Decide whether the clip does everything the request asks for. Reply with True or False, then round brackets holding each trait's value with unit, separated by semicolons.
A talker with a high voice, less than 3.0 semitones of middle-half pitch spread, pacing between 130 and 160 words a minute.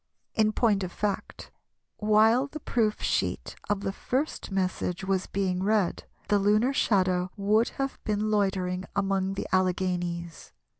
True (200 Hz; 2.4 semitones; 140 wpm)